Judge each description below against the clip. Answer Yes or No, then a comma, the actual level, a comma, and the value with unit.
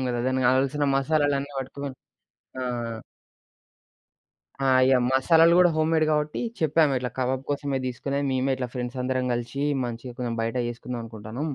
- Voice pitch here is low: Yes, low, 130 Hz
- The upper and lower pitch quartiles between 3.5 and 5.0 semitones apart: No, narrow, 2.6 semitones